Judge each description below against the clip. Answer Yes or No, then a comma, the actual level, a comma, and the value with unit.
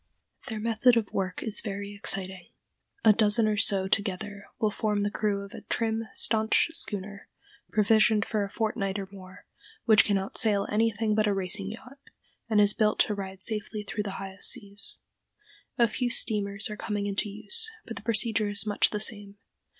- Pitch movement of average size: No, narrow, 1.7 semitones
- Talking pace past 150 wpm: Yes, average, 180 wpm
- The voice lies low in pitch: No, high, 210 Hz